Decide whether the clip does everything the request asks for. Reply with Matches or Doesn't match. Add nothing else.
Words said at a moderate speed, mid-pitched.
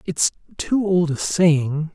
Matches